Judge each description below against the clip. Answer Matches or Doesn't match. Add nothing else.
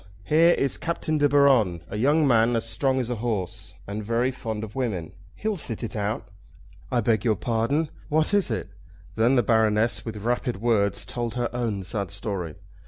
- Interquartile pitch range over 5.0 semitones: Doesn't match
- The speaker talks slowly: Doesn't match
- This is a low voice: Matches